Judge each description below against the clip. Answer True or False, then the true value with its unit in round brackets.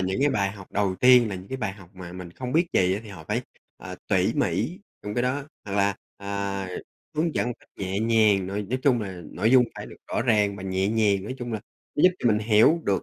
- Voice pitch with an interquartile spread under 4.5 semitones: True (4.0 semitones)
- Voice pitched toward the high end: False (105 Hz)